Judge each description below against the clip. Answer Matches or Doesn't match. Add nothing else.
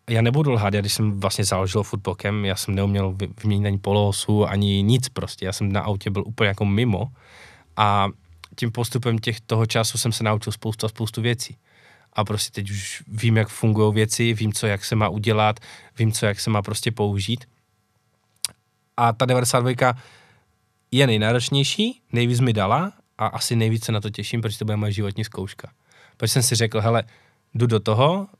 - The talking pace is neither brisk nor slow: Doesn't match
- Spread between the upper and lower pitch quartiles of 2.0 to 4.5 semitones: Matches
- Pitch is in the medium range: Doesn't match